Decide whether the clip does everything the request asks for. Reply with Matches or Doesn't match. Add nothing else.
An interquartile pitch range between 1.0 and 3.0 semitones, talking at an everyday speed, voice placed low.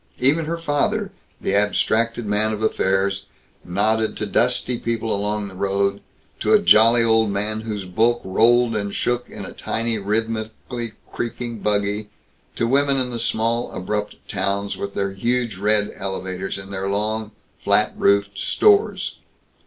Matches